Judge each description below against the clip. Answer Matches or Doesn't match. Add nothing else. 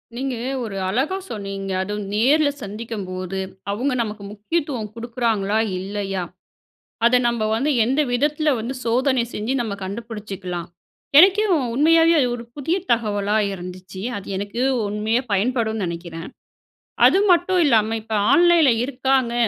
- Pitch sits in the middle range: Doesn't match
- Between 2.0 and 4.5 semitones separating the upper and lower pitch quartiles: Doesn't match